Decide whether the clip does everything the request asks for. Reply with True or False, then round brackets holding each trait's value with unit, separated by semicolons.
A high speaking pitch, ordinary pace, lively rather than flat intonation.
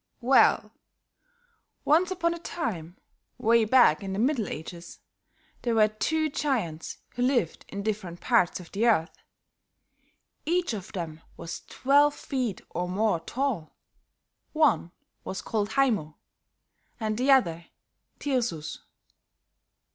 False (220 Hz; 120 wpm; 7.5 semitones)